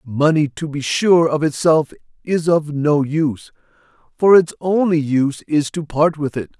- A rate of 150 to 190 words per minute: Yes, average, 175 wpm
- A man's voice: Yes, male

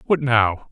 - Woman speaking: No, male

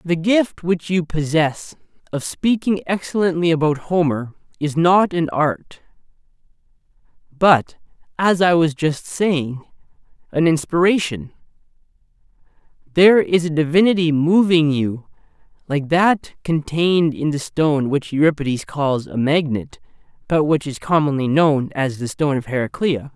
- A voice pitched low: No, medium, 160 Hz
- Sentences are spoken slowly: Yes, slow, 125 wpm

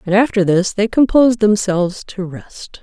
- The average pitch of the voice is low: No, high, 200 Hz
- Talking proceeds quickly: No, average, 170 wpm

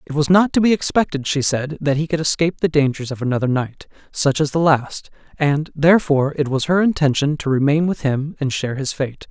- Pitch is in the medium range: Yes, medium, 150 Hz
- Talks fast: Yes, fast, 225 wpm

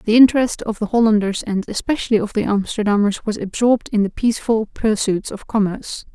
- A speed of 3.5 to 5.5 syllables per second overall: No, 6.0 syllables/s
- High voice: Yes, high, 215 Hz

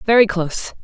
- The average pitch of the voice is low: No, high, 195 Hz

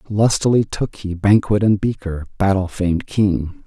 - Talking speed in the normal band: Yes, average, 150 wpm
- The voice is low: Yes, low, 100 Hz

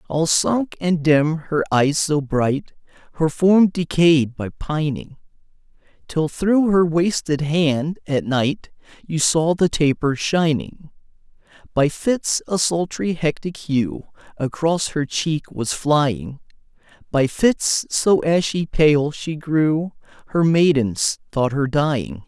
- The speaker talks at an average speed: No, slow, 130 wpm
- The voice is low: No, medium, 155 Hz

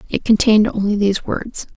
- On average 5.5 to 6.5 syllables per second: Yes, 6.0 syllables/s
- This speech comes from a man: No, female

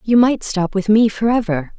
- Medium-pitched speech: No, high, 210 Hz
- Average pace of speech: No, fast, 235 wpm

